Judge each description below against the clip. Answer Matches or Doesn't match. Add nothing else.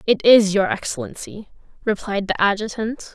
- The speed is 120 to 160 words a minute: Matches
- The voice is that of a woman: Matches